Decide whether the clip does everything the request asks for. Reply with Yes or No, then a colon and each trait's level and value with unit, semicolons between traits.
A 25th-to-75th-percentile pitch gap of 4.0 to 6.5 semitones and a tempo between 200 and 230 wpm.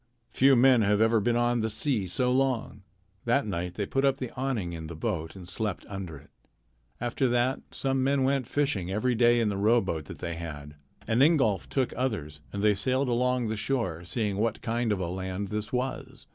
Yes: average, 5.0 semitones; fast, 205 wpm